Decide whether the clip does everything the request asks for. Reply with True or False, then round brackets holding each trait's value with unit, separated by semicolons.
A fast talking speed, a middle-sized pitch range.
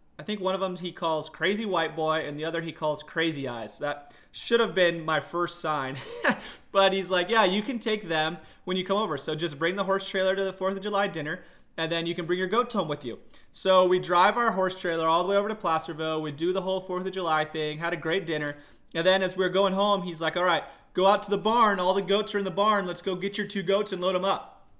True (280 wpm; 3.3 semitones)